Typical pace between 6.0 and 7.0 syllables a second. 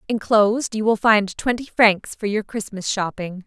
No: 4.6 syllables/s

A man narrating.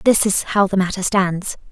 No: female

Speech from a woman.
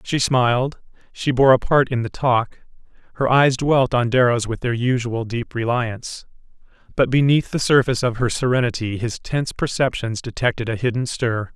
No: male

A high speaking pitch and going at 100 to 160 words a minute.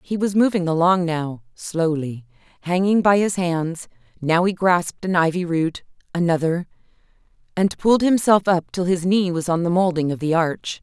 No: medium, 175 Hz; average, 155 wpm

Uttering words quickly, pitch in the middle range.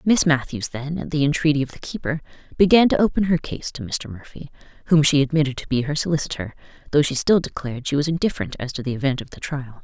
Yes: fast, 230 wpm; medium, 145 Hz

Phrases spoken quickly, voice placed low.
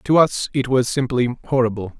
No: average, 180 wpm; low, 125 Hz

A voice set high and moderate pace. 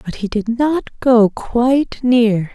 Yes: high, 235 Hz; average, 165 wpm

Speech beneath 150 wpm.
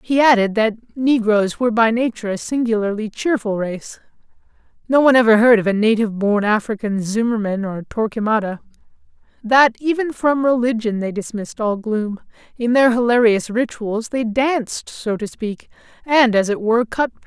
No: average, 165 wpm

